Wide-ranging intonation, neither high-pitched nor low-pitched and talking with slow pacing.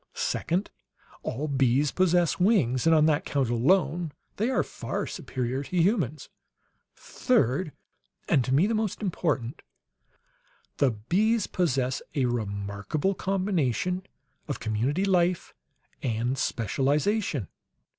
Yes: wide, 6.6 semitones; medium, 150 Hz; slow, 115 wpm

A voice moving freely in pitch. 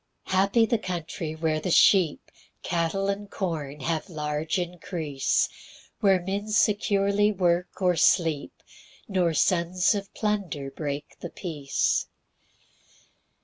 No: average, 3.9 semitones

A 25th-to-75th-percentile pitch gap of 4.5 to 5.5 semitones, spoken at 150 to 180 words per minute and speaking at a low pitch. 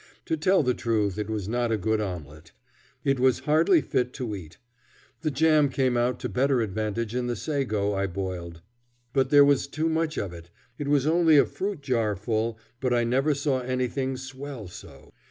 No: average, 5.1 semitones; average, 190 wpm; low, 125 Hz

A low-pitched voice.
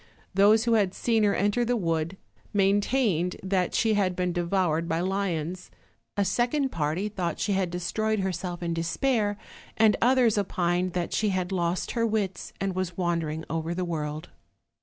No: medium, 185 Hz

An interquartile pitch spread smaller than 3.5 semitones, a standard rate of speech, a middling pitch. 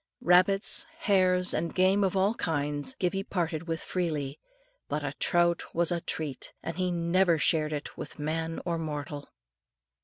Yes: average, 2.9 semitones; average, 155 wpm; medium, 170 Hz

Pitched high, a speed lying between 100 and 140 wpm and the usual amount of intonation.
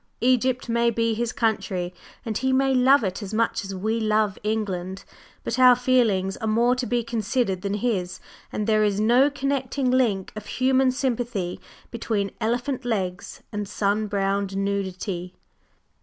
No: high, 220 Hz; average, 155 wpm; average, 3.8 semitones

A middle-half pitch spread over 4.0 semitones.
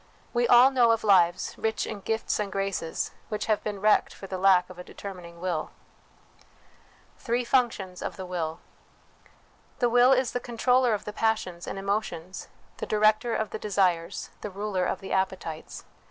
No: average, 3.5 semitones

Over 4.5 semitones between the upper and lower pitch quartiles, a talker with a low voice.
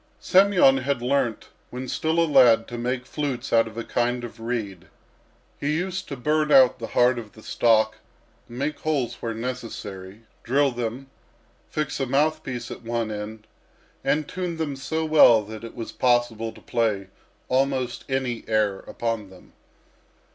No: average, 3.8 semitones; low, 125 Hz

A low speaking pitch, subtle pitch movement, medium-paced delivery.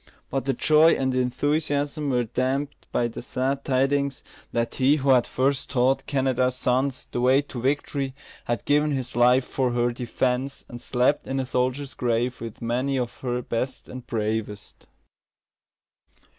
Yes: low, 130 Hz; narrow, 2.0 semitones; average, 155 wpm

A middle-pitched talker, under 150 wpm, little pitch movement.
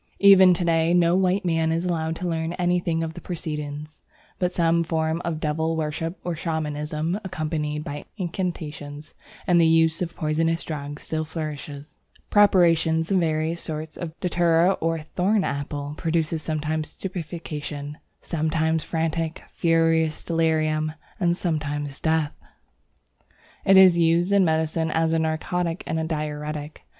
Yes: medium, 160 Hz; average, 140 wpm; narrow, 1.7 semitones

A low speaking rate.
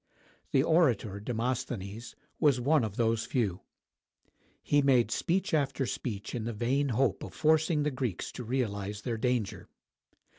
No: average, 145 wpm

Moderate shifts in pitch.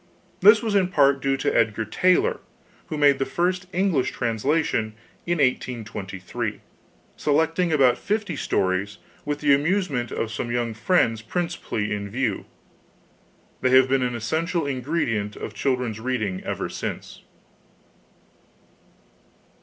No: wide, 6.8 semitones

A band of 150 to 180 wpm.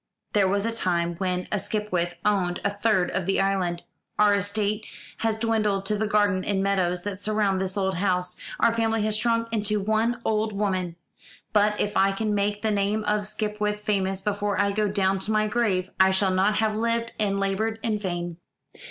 No: average, 195 wpm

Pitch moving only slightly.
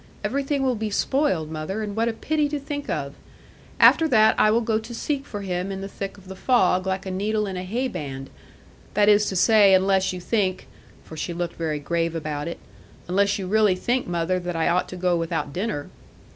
No: average, 3.9 semitones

